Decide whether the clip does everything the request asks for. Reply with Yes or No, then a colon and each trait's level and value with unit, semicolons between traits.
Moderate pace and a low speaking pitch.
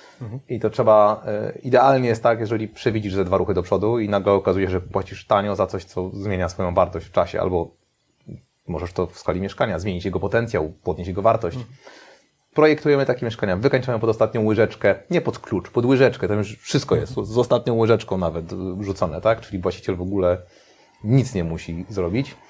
No: fast, 185 wpm; low, 105 Hz